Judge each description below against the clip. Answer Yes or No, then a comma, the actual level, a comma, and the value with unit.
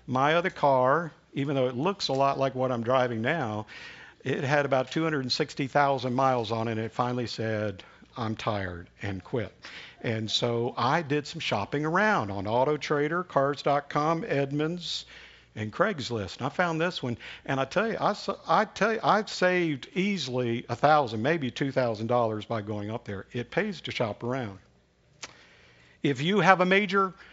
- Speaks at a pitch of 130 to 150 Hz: Yes, low, 135 Hz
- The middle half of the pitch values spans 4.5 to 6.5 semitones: Yes, wide, 5.5 semitones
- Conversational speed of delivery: Yes, average, 170 wpm